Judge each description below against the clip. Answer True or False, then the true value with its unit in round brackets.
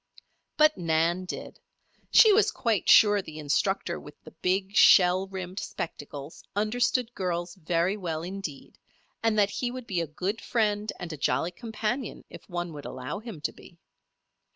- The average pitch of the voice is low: False (190 Hz)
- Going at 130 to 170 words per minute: True (160 wpm)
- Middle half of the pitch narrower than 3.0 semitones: False (4.1 semitones)